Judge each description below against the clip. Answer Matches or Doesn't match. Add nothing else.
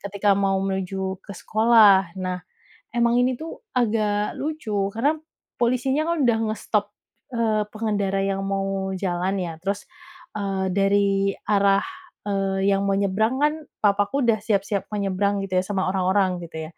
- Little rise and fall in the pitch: Matches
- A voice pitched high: Matches